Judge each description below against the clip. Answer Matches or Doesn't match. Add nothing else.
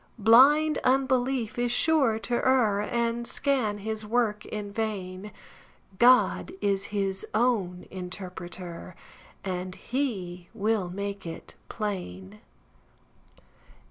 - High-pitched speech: Matches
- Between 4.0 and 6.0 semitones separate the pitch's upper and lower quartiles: Matches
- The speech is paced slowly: Matches